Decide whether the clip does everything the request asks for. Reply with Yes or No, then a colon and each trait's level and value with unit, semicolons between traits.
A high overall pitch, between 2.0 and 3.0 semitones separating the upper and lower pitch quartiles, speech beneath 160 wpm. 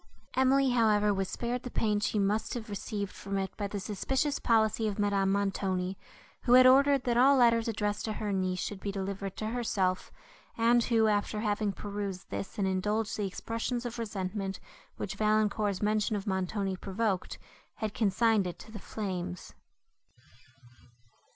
No: high, 210 Hz; average, 2.7 semitones; average, 165 wpm